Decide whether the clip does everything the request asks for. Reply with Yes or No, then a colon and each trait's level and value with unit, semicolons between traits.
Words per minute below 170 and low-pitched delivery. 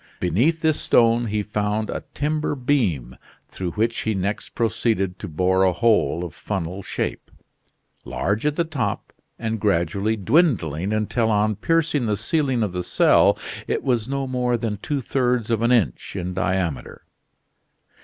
Yes: average, 155 wpm; low, 110 Hz